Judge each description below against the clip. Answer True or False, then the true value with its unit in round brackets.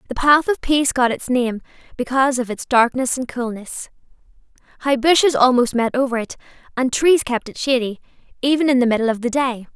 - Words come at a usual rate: True (190 wpm)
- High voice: True (255 Hz)